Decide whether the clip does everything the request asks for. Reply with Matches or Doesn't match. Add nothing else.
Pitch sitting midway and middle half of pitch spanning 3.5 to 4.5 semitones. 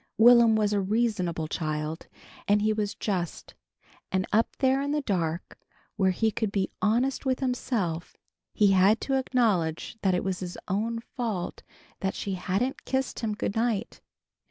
Doesn't match